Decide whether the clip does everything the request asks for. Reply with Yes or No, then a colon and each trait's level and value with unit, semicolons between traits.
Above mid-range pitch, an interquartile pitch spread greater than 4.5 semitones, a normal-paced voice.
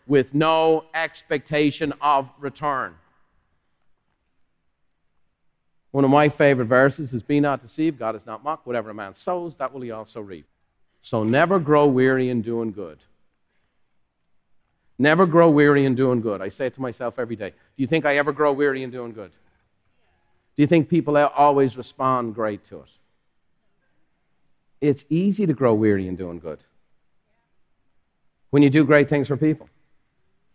No: low, 135 Hz; average, 5.0 semitones; average, 160 wpm